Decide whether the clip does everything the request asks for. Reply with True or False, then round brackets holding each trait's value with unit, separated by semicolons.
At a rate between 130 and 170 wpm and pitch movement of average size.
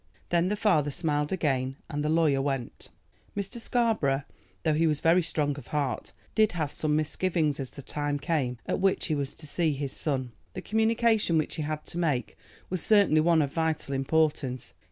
False (190 wpm; 3.4 semitones)